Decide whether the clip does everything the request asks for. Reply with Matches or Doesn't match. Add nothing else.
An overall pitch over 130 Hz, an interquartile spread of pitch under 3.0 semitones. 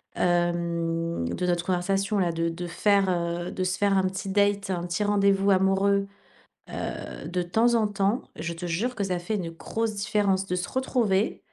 Matches